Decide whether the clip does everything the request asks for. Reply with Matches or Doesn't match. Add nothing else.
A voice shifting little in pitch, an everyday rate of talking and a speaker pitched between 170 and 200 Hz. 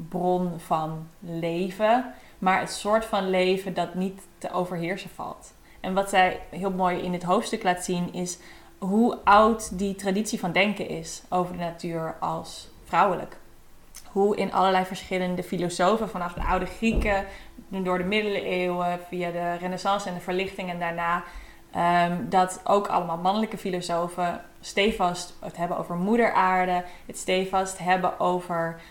Matches